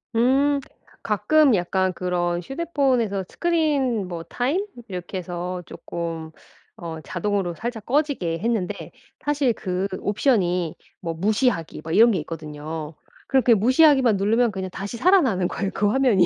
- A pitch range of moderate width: No, wide, 6.6 semitones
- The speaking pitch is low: No, high, 205 Hz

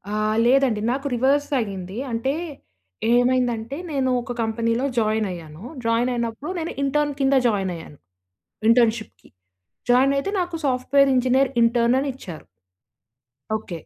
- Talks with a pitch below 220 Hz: No, high, 245 Hz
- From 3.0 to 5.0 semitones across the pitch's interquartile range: Yes, average, 3.6 semitones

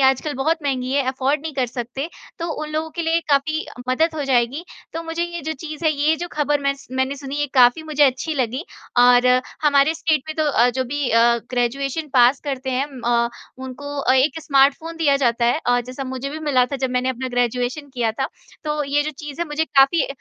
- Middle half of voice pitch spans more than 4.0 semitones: No, average, 3.2 semitones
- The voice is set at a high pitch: Yes, very high, 275 Hz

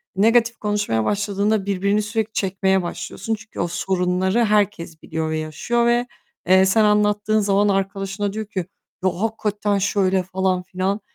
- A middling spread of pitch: No, narrow, 2.0 semitones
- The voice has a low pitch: No, high, 200 Hz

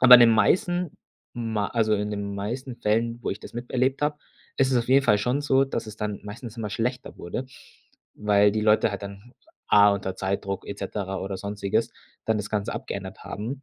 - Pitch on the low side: Yes, low, 110 Hz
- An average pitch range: Yes, average, 3.5 semitones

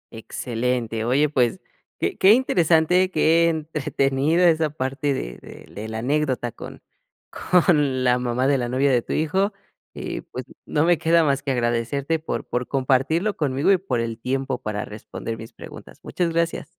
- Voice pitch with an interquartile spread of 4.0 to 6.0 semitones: Yes, average, 4.8 semitones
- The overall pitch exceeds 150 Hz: No, medium, 140 Hz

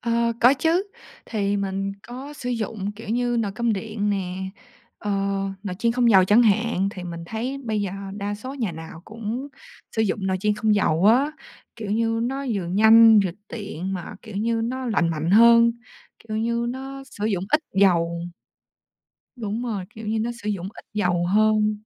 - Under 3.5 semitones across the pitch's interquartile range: Yes, average, 3.1 semitones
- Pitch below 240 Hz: Yes, high, 215 Hz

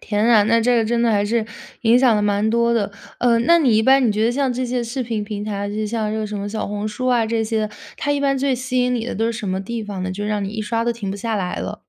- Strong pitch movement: No, narrow, 2.6 semitones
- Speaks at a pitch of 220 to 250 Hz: Yes, high, 225 Hz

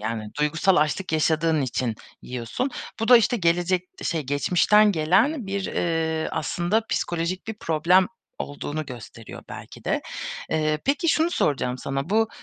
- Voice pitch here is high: No, medium, 165 Hz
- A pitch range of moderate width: Yes, average, 4.8 semitones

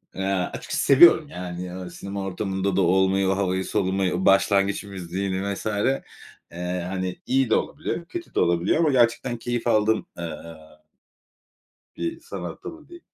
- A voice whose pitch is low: Yes, low, 100 Hz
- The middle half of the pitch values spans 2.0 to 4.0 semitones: No, average, 4.4 semitones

